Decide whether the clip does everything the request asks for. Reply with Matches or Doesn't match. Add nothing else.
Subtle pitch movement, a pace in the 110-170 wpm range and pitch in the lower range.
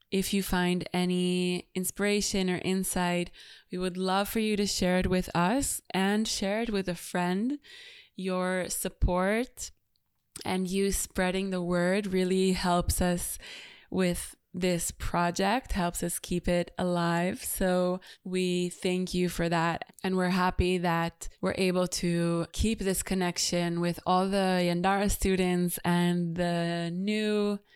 Doesn't match